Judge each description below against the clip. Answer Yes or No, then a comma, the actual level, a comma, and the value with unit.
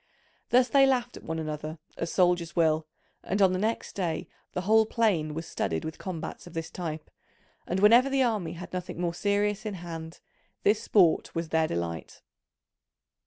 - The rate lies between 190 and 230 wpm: No, average, 175 wpm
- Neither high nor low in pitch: Yes, medium, 175 Hz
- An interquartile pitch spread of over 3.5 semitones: Yes, average, 4.5 semitones